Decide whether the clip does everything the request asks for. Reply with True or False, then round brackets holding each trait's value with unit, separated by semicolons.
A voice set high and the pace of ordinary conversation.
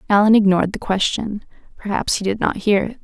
True (205 Hz; 180 wpm)